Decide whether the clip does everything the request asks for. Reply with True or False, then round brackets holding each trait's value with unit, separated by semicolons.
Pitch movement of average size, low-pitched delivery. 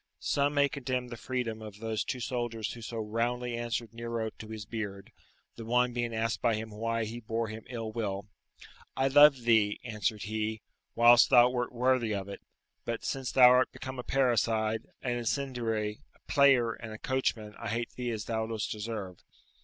False (2.1 semitones; 115 Hz)